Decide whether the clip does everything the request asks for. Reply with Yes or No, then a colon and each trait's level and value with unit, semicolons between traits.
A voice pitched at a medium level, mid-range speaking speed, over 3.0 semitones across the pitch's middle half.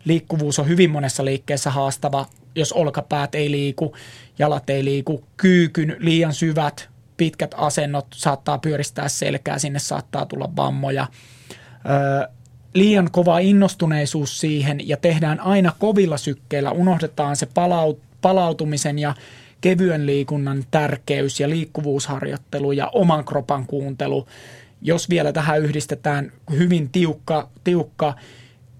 No: medium, 145 Hz; average, 115 wpm; average, 2.7 semitones